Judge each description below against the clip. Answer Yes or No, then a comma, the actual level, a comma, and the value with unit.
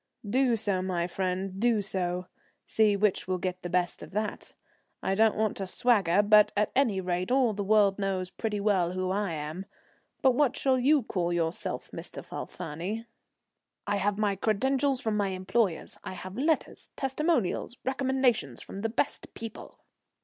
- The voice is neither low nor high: No, high, 205 Hz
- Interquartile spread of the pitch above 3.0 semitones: Yes, average, 4.0 semitones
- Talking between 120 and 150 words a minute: No, average, 165 wpm